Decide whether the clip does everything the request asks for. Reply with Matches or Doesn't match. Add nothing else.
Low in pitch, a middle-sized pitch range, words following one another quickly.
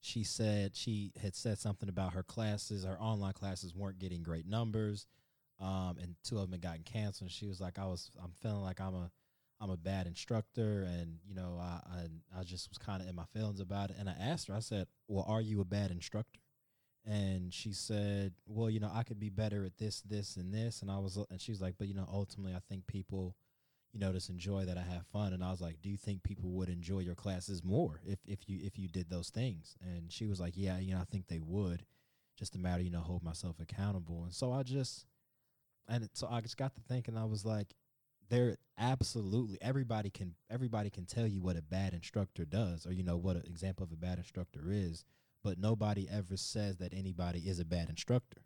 Matches